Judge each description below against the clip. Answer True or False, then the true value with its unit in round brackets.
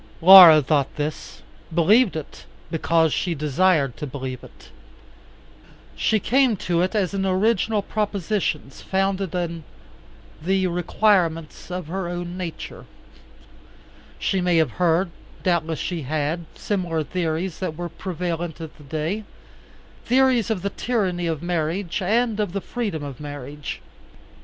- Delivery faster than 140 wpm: False (135 wpm)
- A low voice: False (175 Hz)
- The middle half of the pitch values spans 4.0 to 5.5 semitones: False (3.5 semitones)